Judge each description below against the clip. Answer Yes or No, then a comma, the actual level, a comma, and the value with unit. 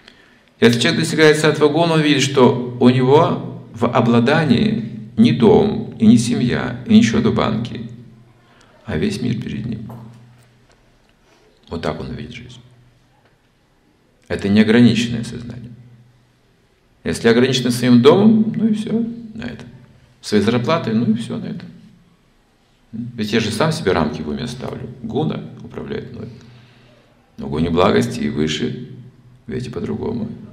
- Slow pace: No, average, 135 wpm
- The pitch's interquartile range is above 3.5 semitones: No, narrow, 2.5 semitones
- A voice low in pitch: Yes, low, 120 Hz